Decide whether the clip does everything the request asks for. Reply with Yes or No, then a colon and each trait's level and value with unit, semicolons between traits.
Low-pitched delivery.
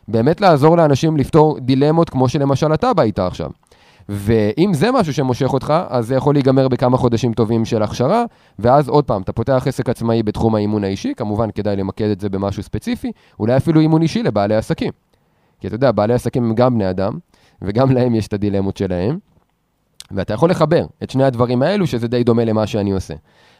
Yes: low, 120 Hz